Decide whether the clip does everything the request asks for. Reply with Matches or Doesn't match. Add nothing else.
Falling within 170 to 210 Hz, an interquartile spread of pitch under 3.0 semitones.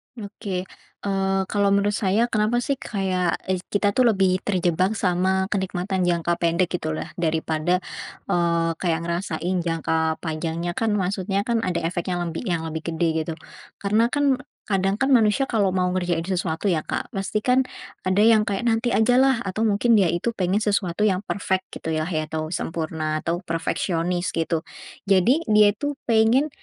Doesn't match